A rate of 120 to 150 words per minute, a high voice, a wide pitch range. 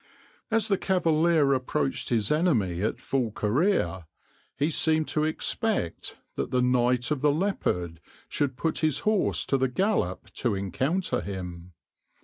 No: average, 140 wpm; low, 135 Hz; wide, 7.5 semitones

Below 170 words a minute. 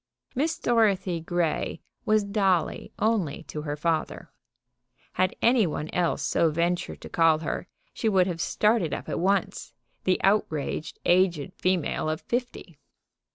Yes: average, 140 wpm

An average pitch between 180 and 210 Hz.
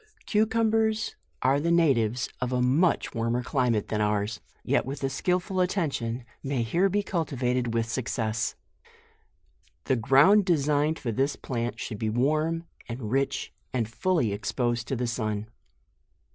No: low, 130 Hz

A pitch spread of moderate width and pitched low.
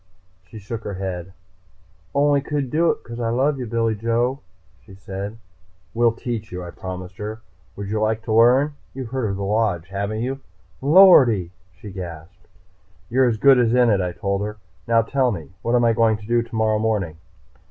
Yes: average, 3.6 semitones; low, 110 Hz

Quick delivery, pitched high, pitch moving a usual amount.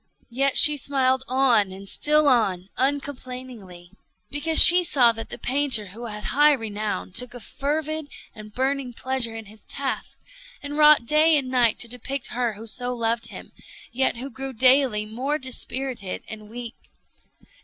No: average, 160 wpm; very high, 250 Hz; average, 3.7 semitones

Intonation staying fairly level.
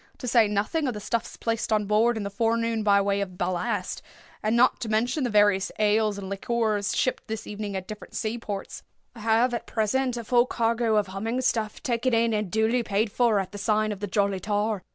Yes: narrow, 2.3 semitones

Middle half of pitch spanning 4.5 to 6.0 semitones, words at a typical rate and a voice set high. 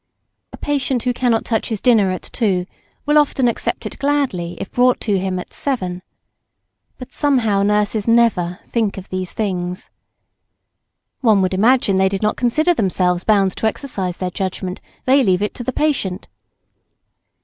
Yes: average, 5.1 semitones; average, 160 wpm; high, 210 Hz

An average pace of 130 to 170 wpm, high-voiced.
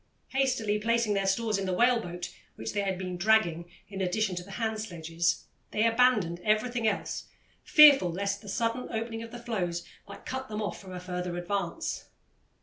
No: average, 185 wpm; high, 205 Hz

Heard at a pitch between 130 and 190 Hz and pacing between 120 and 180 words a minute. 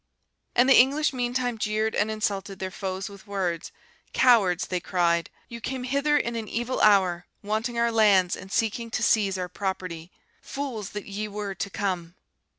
No: high, 210 Hz; average, 170 wpm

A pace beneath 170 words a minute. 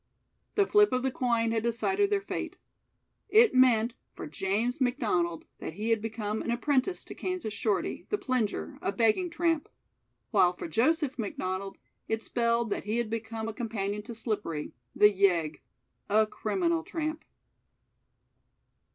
Yes: average, 150 wpm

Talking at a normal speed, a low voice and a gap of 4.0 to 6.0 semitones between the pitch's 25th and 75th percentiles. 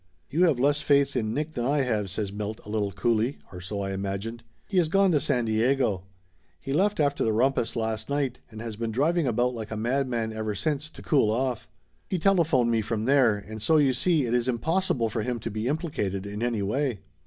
No: fast, 220 wpm; low, 120 Hz; average, 4.6 semitones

